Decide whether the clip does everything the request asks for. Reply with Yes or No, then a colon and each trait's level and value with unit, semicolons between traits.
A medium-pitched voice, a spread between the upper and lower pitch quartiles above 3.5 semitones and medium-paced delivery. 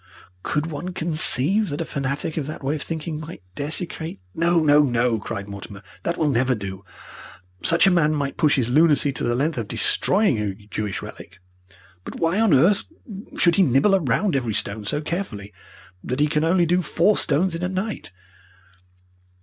Yes: medium, 150 Hz; wide, 5.6 semitones; average, 185 wpm